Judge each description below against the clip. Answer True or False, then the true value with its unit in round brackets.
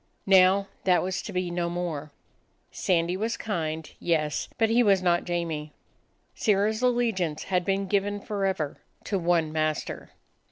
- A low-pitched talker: False (185 Hz)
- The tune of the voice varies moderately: True (3.2 semitones)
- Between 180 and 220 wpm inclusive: False (145 wpm)